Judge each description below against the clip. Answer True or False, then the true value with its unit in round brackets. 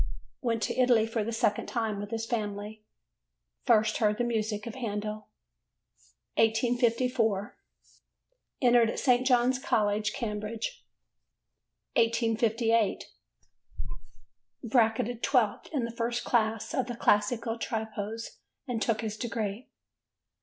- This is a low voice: False (225 Hz)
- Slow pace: True (110 wpm)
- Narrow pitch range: True (2.0 semitones)